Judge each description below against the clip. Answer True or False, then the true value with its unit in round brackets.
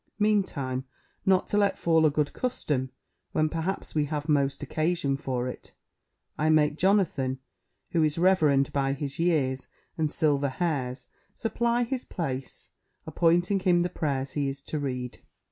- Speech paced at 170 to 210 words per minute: False (150 wpm)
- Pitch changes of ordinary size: True (4.4 semitones)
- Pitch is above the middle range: False (155 Hz)